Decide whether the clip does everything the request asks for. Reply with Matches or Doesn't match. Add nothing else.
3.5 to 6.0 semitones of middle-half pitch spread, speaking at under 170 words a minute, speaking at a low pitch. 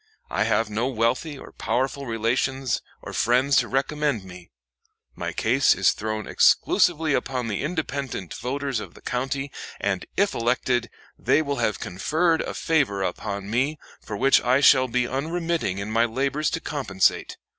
Matches